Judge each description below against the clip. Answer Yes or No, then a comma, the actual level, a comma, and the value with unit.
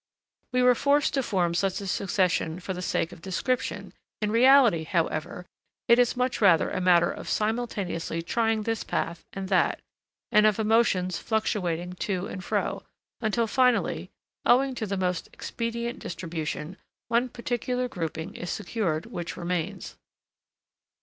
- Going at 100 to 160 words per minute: Yes, average, 145 wpm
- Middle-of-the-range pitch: No, high, 200 Hz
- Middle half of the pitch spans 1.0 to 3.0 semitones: No, average, 5.0 semitones